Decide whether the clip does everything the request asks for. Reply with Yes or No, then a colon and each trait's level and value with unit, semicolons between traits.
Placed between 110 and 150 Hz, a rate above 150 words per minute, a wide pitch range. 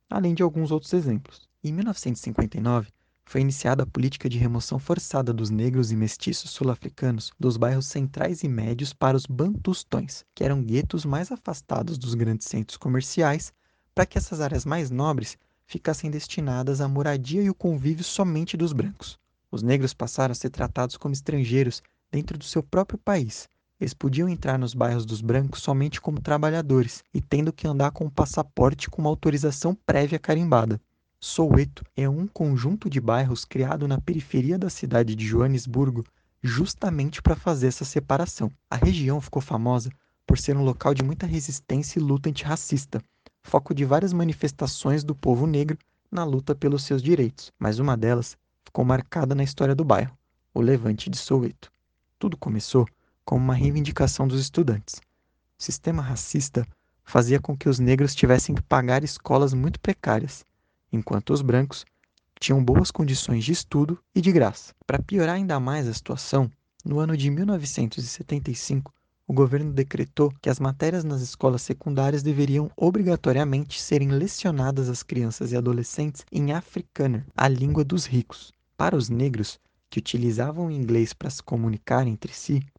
No: medium, 140 Hz; average, 160 wpm; average, 3.8 semitones